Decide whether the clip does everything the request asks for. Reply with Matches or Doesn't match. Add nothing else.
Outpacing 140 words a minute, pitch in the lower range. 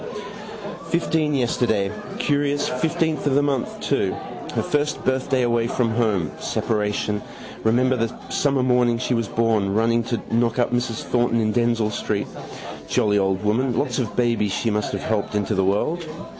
Matches